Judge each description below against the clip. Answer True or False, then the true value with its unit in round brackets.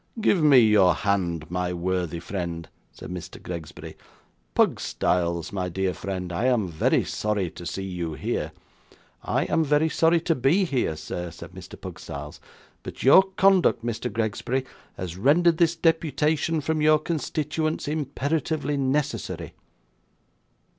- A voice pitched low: True (115 Hz)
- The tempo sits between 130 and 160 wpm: True (135 wpm)